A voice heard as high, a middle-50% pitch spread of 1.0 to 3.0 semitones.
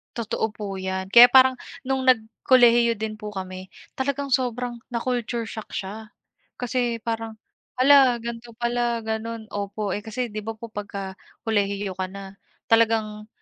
Yes: high, 225 Hz; average, 2.7 semitones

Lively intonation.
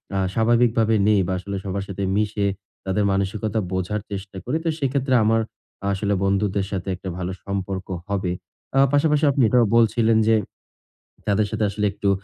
No: narrow, 2.6 semitones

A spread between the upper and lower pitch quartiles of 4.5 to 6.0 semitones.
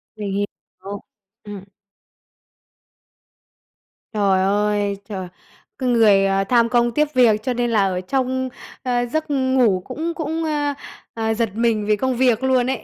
No: average, 4.0 semitones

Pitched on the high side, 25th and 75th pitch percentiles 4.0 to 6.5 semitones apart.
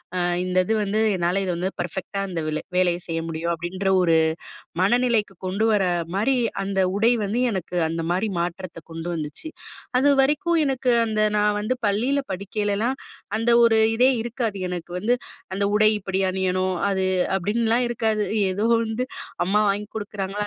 No: high, 200 Hz; average, 3.5 semitones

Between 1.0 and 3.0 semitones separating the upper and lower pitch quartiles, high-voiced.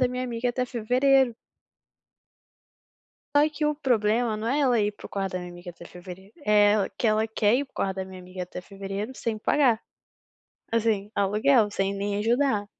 No: average, 3.9 semitones; high, 215 Hz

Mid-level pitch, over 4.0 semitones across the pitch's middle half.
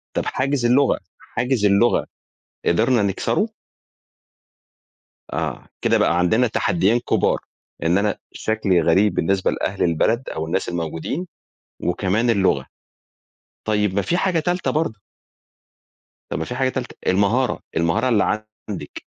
No: low, 105 Hz; wide, 5.5 semitones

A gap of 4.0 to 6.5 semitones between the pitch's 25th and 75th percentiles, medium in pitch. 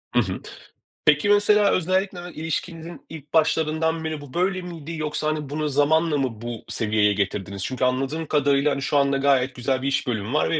No: average, 3.5 semitones; medium, 150 Hz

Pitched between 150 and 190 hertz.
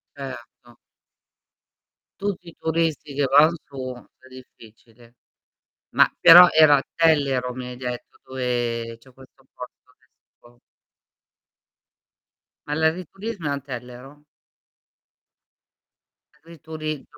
No: low, 135 Hz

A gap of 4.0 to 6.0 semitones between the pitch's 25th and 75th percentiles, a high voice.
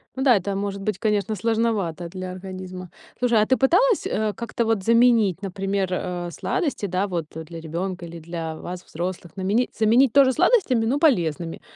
Yes: average, 4.5 semitones; high, 195 Hz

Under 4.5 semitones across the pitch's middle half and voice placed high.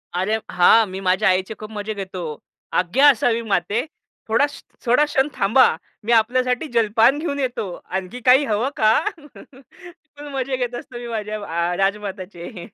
No: average, 4.8 semitones; high, 225 Hz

